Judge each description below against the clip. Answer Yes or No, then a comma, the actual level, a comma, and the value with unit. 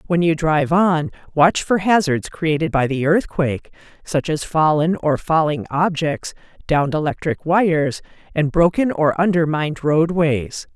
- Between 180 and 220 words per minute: No, average, 140 wpm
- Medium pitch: Yes, medium, 160 Hz